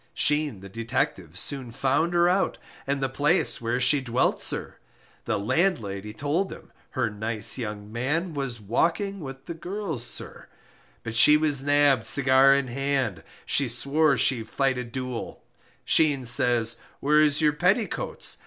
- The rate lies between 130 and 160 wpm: Yes, average, 155 wpm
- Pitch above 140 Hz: No, low, 135 Hz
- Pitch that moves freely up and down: No, average, 4.4 semitones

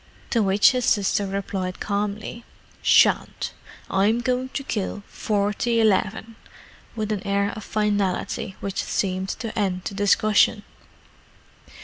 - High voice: Yes, high, 205 Hz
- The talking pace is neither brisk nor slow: No, slow, 120 wpm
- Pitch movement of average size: No, narrow, 1.9 semitones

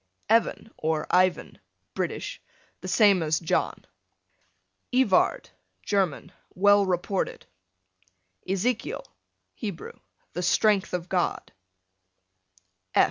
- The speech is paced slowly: Yes, slow, 80 wpm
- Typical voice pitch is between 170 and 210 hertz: Yes, high, 190 Hz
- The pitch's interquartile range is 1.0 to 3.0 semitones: Yes, average, 2.7 semitones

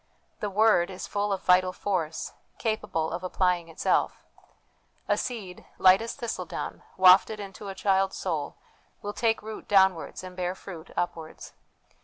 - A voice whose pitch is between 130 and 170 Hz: No, high, 190 Hz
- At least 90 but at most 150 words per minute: Yes, average, 145 wpm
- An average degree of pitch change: No, narrow, 2.3 semitones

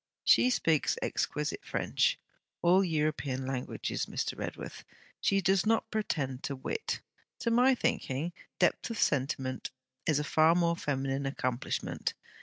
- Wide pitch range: Yes, wide, 5.9 semitones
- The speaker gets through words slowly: Yes, slow, 130 wpm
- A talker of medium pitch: Yes, medium, 155 Hz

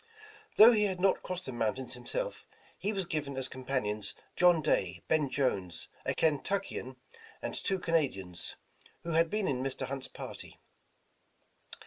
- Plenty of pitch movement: Yes, wide, 6.3 semitones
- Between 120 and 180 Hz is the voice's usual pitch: Yes, medium, 140 Hz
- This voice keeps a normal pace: Yes, average, 150 wpm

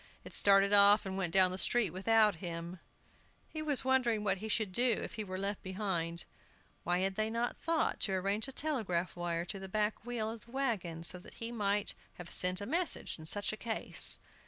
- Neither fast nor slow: No, fast, 210 wpm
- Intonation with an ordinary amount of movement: Yes, average, 3.7 semitones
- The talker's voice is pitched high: Yes, high, 200 Hz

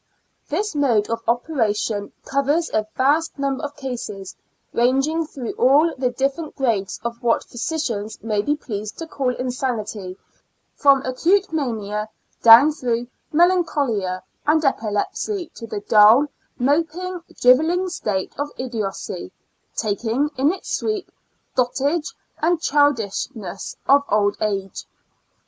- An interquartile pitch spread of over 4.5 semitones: Yes, wide, 5.6 semitones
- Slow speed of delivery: Yes, slow, 120 wpm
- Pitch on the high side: Yes, very high, 255 Hz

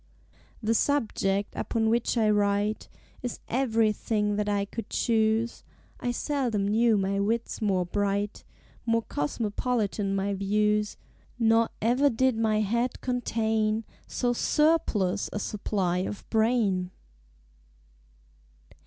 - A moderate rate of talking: No, slow, 110 wpm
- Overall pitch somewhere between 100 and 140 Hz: No, high, 215 Hz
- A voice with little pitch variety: Yes, narrow, 2.3 semitones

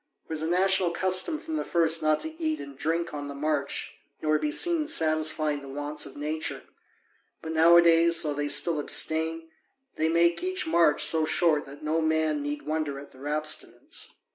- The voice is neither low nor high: Yes, medium, 160 Hz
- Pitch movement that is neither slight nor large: No, narrow, 2.3 semitones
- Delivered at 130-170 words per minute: No, average, 185 wpm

